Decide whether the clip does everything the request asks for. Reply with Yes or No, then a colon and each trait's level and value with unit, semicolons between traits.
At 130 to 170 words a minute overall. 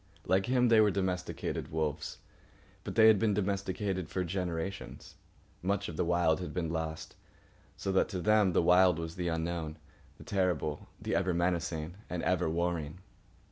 Yes: average, 165 wpm